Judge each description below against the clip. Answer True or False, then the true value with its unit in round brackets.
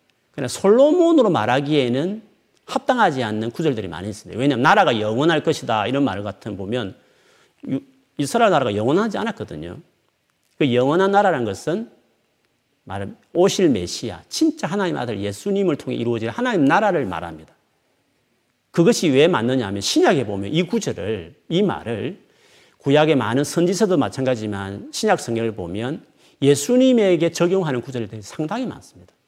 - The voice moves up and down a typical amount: False (9.0 semitones)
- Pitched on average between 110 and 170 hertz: True (140 Hz)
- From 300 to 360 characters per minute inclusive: True (350 characters per minute)